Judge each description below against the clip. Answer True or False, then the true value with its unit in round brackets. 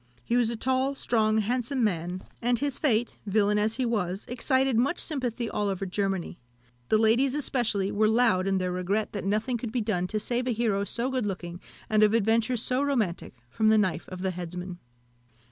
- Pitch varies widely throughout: False (3.9 semitones)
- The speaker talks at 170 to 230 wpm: True (195 wpm)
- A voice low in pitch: False (220 Hz)